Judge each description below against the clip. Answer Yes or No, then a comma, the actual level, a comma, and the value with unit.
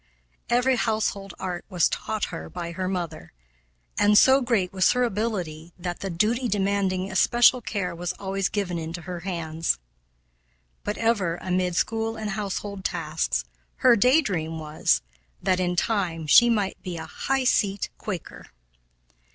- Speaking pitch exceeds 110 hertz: Yes, high, 190 Hz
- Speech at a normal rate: Yes, average, 150 wpm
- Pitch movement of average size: Yes, average, 3.9 semitones